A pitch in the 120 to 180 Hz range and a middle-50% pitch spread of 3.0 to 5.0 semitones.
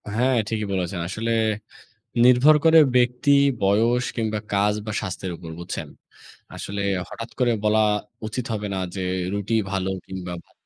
No: low, 110 Hz; average, 3.9 semitones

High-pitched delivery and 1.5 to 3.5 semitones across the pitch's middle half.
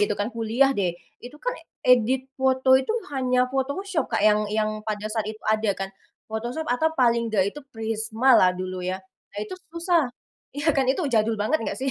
No: high, 235 Hz; average, 3.9 semitones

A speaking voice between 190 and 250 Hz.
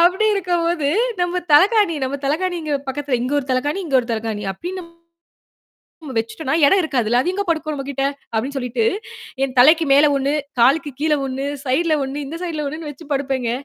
No: very high, 290 Hz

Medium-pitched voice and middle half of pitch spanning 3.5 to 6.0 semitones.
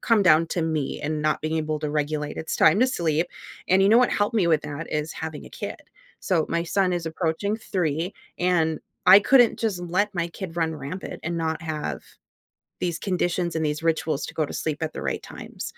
No: medium, 165 Hz; average, 2.9 semitones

